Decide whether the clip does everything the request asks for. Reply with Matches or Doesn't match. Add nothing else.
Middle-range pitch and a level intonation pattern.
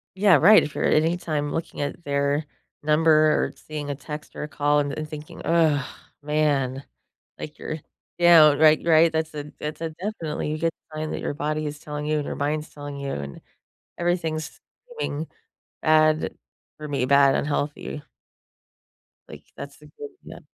Matches